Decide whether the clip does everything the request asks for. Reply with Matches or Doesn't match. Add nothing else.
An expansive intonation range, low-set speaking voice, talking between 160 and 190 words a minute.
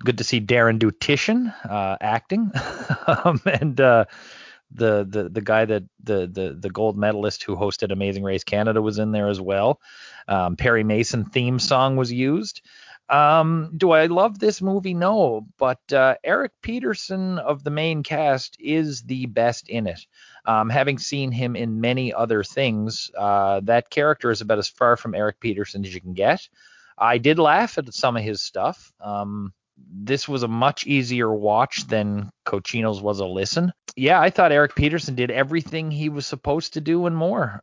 Matches